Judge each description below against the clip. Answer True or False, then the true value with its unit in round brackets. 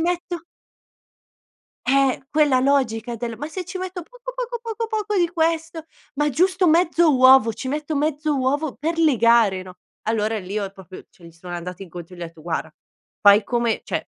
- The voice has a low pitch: False (275 Hz)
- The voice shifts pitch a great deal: True (7.7 semitones)